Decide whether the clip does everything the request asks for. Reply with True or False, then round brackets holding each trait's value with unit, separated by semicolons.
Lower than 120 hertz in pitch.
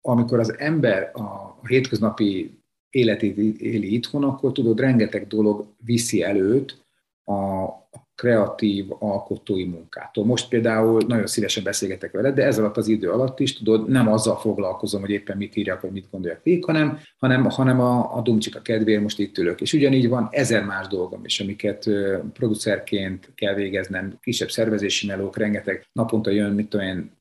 True (110 Hz)